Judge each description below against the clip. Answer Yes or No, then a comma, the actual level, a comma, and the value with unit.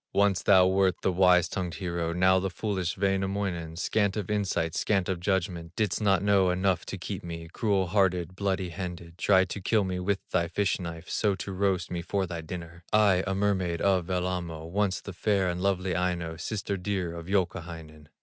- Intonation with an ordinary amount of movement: No, narrow, 2.2 semitones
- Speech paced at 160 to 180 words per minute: No, average, 190 wpm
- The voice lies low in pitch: Yes, very low, 95 Hz